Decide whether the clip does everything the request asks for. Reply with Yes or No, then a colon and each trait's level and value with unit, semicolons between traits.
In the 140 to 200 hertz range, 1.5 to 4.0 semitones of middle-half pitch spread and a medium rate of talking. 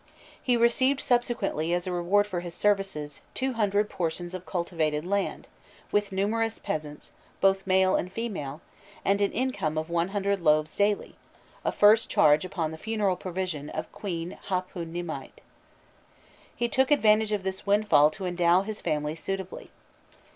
Yes: high, 190 Hz; average, 3.6 semitones; average, 150 wpm